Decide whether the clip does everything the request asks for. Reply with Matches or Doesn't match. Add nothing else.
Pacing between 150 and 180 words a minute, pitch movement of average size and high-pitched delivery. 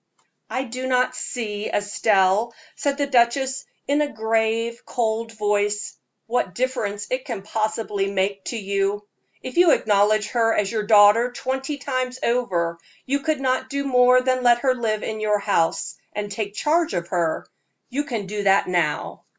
Matches